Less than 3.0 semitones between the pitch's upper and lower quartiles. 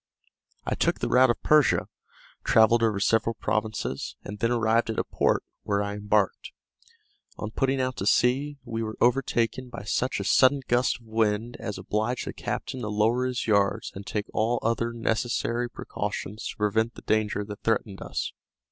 Yes: narrow, 2.4 semitones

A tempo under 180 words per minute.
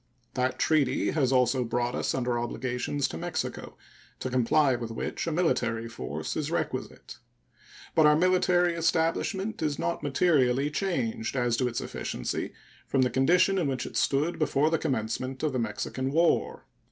Yes: average, 160 wpm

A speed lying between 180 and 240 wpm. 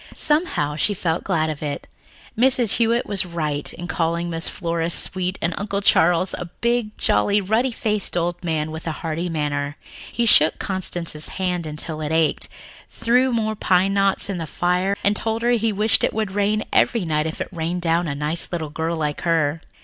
Yes: average, 195 wpm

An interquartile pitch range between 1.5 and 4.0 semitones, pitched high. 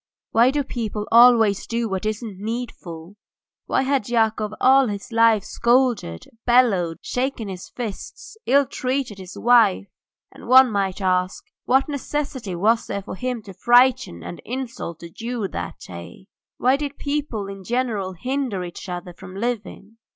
No: average, 4.6 semitones; high, 225 Hz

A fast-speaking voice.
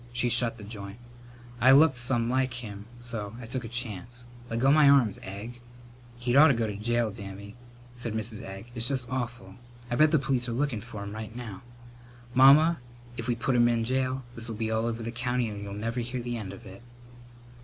Yes: fast, 210 wpm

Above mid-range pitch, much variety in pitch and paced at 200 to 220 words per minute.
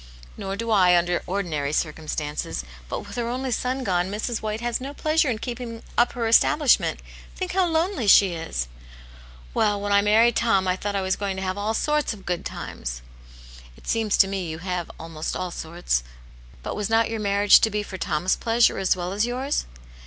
No: high, 200 Hz; average, 4.8 semitones; fast, 205 wpm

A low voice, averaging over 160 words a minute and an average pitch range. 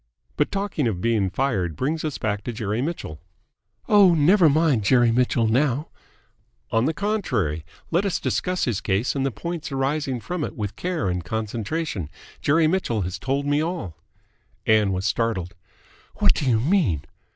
No: low, 130 Hz; average, 170 wpm; wide, 7.4 semitones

